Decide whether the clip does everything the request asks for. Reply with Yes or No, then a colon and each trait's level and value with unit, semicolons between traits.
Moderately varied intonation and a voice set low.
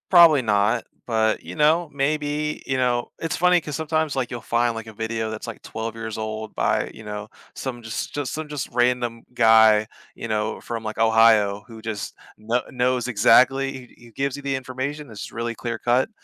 Yes: average, 3.6 semitones; low, 120 Hz